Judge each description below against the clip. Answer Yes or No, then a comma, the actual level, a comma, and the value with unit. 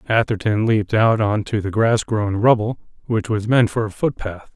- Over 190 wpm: Yes, average, 200 wpm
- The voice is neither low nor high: No, low, 110 Hz